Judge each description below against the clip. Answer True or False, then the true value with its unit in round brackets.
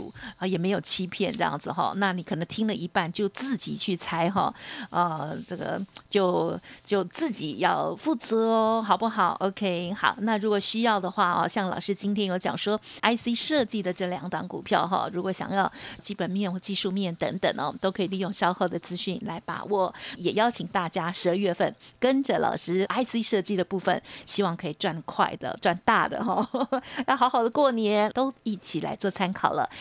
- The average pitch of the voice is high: True (200 Hz)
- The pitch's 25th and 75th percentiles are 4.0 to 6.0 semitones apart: False (3.3 semitones)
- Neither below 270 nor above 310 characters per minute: True (285 characters per minute)